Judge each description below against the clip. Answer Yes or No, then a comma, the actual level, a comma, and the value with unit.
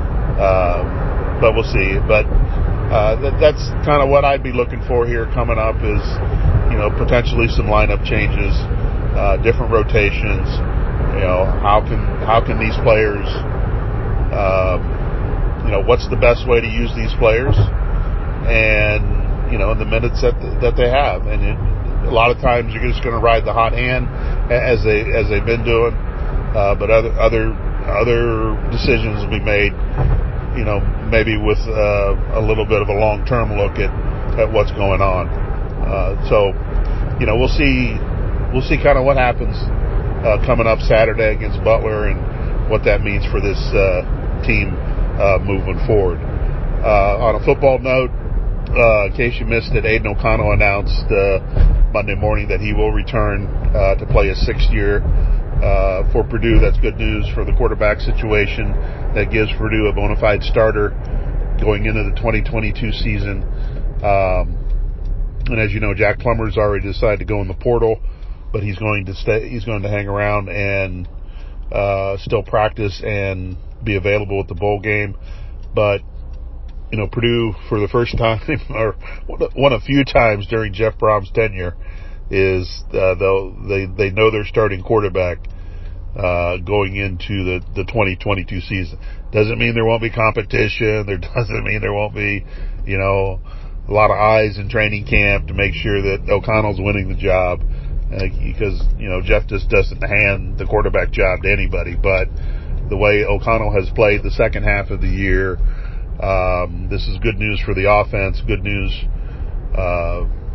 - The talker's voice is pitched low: Yes, low, 105 Hz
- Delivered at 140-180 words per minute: Yes, average, 170 wpm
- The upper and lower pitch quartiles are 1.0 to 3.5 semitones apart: Yes, average, 2.8 semitones